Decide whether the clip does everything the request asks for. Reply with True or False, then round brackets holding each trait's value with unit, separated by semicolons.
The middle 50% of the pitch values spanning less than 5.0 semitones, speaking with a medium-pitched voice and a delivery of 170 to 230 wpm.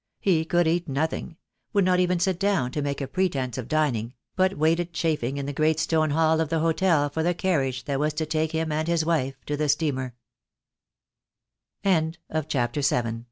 True (2.9 semitones; 155 Hz; 180 wpm)